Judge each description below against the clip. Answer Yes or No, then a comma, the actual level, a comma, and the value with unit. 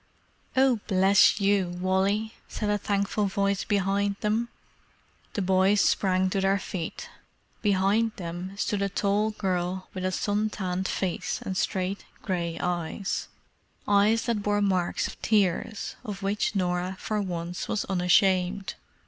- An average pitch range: No, narrow, 1.9 semitones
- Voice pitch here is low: No, high, 195 Hz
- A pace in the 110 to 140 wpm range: Yes, slow, 135 wpm